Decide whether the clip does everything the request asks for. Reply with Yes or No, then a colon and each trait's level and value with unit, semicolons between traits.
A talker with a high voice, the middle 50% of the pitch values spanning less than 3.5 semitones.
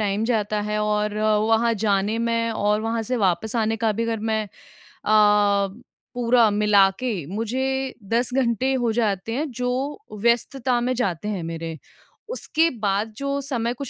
Yes: high, 225 Hz; average, 2.7 semitones